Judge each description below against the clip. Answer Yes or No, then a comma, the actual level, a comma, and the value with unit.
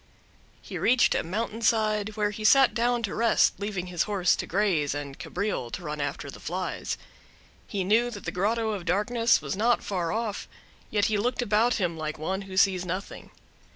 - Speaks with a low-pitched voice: No, high, 205 Hz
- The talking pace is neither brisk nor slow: Yes, average, 190 wpm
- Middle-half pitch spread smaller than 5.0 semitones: Yes, average, 3.7 semitones